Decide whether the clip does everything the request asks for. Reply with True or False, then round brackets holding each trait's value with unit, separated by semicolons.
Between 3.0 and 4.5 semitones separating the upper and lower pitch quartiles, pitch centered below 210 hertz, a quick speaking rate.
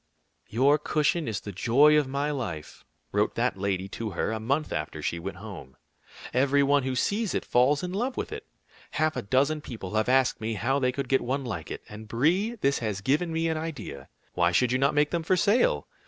False (5.6 semitones; 135 Hz; 220 wpm)